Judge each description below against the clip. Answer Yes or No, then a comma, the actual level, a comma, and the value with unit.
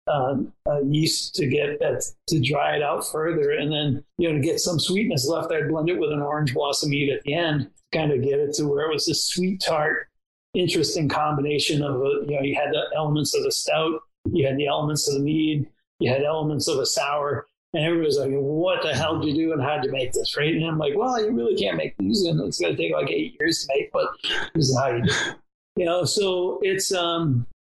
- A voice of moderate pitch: Yes, medium, 155 Hz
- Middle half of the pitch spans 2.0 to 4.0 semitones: No, average, 4.8 semitones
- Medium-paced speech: No, fast, 250 wpm